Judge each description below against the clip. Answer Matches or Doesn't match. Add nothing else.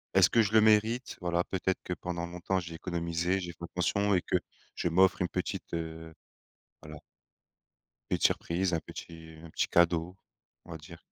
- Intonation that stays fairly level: Matches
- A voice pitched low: Matches